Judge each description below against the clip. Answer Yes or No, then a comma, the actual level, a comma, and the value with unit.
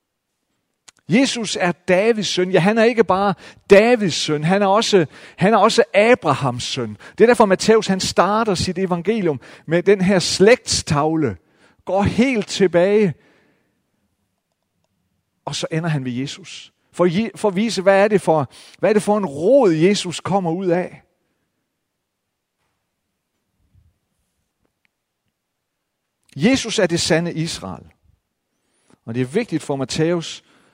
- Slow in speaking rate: Yes, slow, 135 wpm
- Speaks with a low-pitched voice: No, medium, 180 Hz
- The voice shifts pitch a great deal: Yes, wide, 6.2 semitones